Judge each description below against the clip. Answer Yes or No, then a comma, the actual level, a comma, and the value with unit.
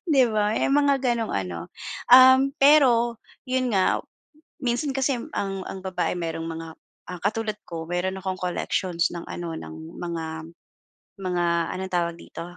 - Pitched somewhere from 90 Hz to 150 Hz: No, high, 190 Hz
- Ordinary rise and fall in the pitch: No, wide, 6.4 semitones